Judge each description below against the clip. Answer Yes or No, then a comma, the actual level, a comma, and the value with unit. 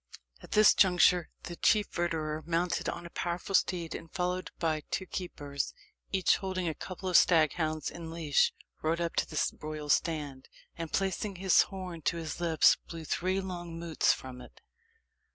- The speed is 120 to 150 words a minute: No, average, 170 wpm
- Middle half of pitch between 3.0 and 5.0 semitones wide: No, narrow, 2.5 semitones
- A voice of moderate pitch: Yes, medium, 170 Hz